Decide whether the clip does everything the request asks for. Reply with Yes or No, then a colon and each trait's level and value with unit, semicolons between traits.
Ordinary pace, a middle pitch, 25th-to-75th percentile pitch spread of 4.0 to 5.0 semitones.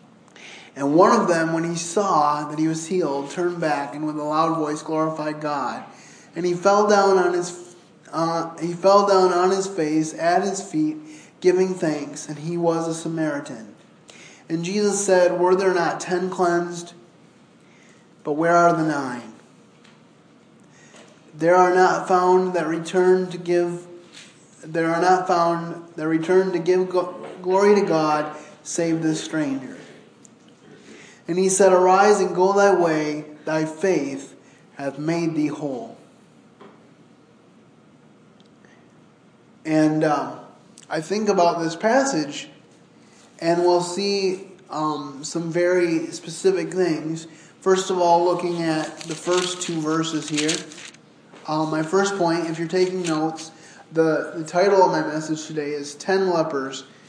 No: average, 145 wpm; medium, 170 Hz; average, 2.7 semitones